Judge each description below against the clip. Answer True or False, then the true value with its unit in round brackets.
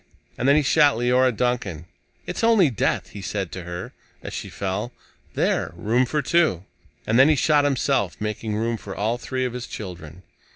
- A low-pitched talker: True (120 Hz)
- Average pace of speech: True (190 wpm)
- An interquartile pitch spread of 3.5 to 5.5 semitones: True (5.2 semitones)